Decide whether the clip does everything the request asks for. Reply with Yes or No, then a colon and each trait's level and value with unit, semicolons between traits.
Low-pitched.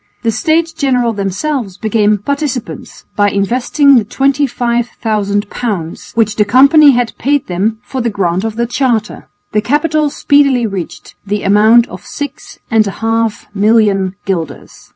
No: high, 225 Hz